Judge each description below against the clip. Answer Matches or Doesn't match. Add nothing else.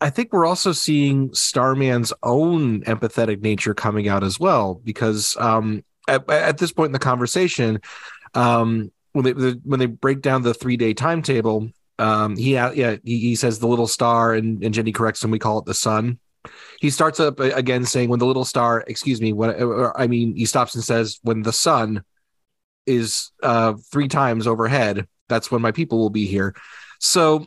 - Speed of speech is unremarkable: Matches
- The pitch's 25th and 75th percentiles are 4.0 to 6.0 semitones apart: Doesn't match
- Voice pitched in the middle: Doesn't match